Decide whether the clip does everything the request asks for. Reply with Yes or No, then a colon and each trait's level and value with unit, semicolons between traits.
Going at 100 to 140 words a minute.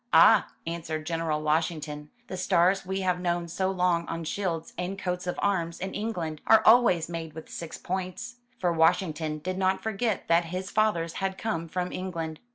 No: average, 175 wpm